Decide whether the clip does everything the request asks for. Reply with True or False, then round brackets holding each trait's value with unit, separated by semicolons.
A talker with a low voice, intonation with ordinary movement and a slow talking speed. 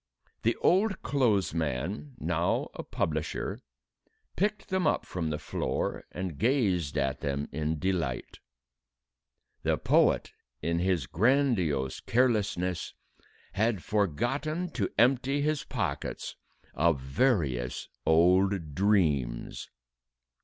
False (95 Hz; 7.8 semitones; 105 wpm)